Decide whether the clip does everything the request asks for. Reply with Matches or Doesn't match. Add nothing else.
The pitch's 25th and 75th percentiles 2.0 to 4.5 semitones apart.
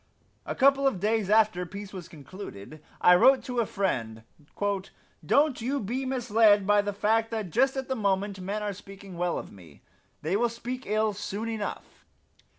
Matches